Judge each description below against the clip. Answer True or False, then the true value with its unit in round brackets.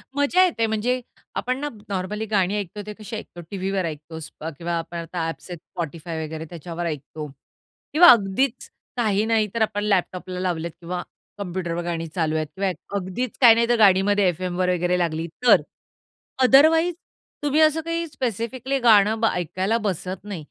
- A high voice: True (195 Hz)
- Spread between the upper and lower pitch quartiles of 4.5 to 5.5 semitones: True (5.0 semitones)